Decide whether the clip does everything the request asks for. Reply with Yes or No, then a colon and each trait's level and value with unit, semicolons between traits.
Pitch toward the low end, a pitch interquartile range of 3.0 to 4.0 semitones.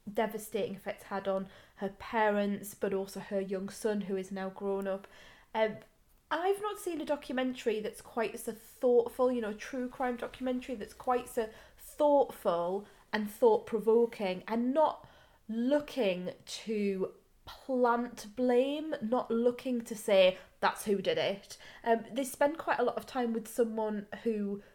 No: high, 225 Hz; average, 3.7 semitones